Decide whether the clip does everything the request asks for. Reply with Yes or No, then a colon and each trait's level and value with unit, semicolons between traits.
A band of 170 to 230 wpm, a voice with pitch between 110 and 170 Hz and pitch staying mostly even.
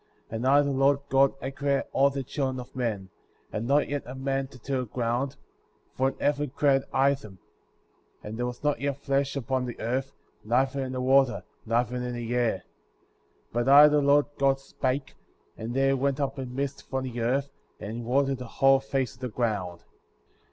Yes: average, 200 wpm; low, 135 Hz; narrow, 2.1 semitones